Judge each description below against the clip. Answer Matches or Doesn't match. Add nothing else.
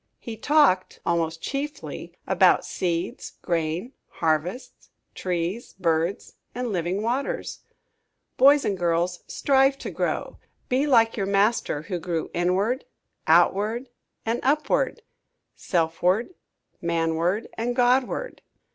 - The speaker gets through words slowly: Matches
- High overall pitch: Matches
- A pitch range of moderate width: Doesn't match